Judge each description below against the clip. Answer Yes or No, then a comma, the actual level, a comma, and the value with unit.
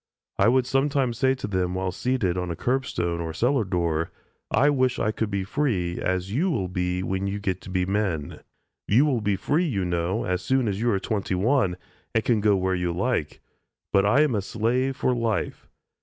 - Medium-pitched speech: No, low, 100 Hz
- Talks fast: Yes, fast, 215 wpm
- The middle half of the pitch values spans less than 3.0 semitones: No, wide, 5.6 semitones